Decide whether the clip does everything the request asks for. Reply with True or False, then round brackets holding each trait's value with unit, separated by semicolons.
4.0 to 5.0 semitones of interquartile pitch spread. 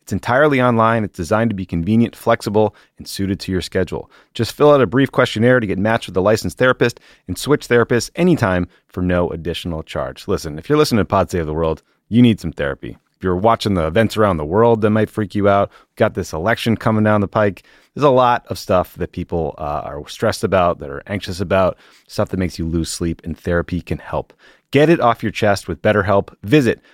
True (4.4 semitones)